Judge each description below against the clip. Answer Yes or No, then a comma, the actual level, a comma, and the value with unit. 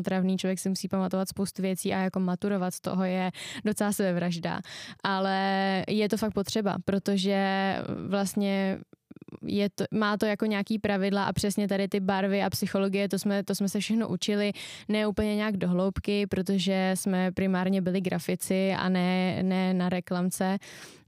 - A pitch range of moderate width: No, narrow, 1.4 semitones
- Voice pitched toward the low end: No, high, 195 Hz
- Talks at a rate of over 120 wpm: Yes, average, 165 wpm